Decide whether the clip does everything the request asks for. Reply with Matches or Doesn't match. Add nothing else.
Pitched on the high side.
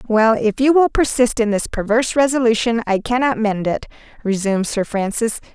Matches